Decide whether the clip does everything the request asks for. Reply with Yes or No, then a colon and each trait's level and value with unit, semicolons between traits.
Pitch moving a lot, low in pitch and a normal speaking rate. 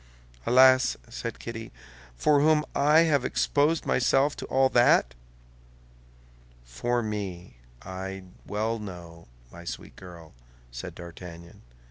No: wide, 7.2 semitones; low, 110 Hz; slow, 110 wpm